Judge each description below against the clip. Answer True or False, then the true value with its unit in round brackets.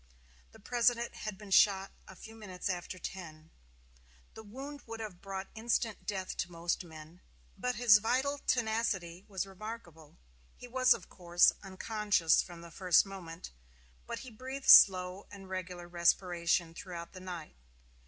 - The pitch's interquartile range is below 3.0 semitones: False (4.1 semitones)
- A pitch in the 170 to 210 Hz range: True (190 Hz)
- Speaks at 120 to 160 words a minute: True (155 wpm)